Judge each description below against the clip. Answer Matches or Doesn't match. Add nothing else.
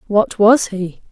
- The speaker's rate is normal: Matches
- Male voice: Doesn't match